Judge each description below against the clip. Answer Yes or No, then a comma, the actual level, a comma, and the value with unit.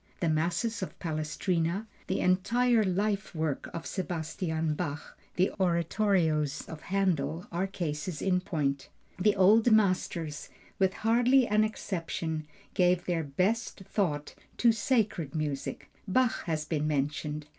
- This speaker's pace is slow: Yes, slow, 125 wpm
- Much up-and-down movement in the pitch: No, average, 4.4 semitones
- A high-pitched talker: No, medium, 175 Hz